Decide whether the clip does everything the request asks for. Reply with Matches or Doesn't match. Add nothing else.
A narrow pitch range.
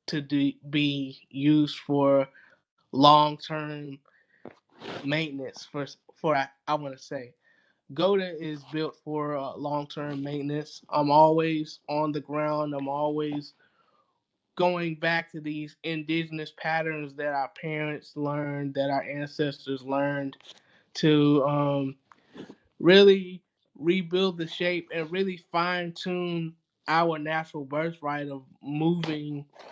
Matches